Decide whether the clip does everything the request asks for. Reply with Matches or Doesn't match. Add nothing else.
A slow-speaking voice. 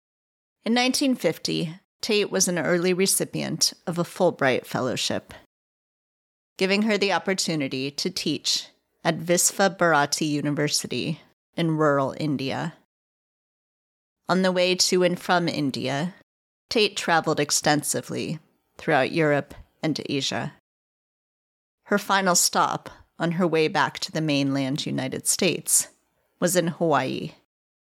Matches